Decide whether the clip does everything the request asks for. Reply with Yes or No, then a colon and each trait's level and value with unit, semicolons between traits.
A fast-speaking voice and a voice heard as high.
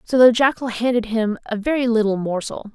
No: average, 195 wpm; high, 230 Hz